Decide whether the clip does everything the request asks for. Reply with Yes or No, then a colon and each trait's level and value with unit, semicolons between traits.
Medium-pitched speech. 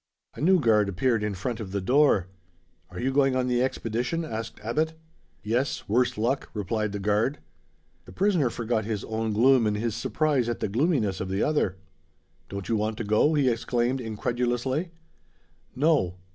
No: low, 120 Hz